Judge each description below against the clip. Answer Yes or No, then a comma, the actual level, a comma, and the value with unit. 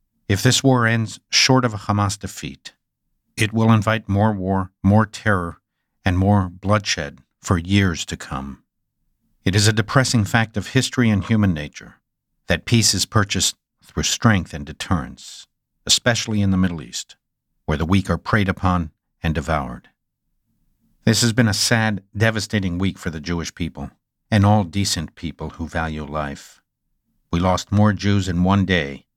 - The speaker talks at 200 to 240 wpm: No, average, 165 wpm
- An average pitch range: Yes, average, 4.4 semitones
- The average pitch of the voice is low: Yes, low, 100 Hz